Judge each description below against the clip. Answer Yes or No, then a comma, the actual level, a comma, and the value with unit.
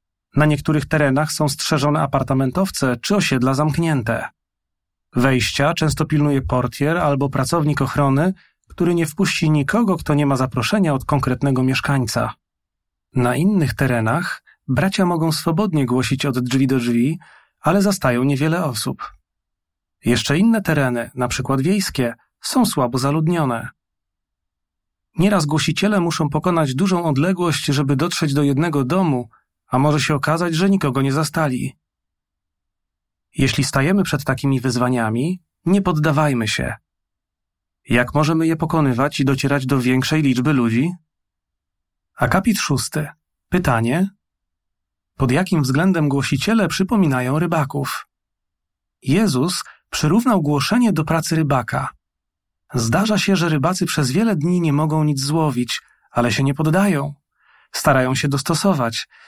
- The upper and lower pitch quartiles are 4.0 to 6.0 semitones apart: Yes, average, 4.8 semitones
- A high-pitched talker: No, medium, 140 Hz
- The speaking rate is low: No, average, 125 wpm